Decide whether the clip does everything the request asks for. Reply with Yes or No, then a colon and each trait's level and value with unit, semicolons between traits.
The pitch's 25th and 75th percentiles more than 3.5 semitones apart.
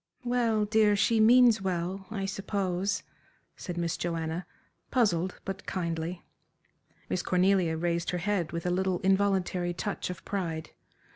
No: average, 2.8 semitones